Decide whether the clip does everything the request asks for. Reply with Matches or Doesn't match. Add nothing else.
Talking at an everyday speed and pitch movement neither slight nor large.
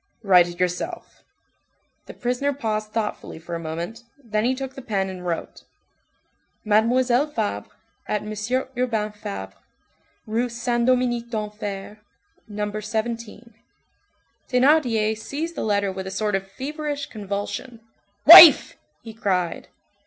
Doesn't match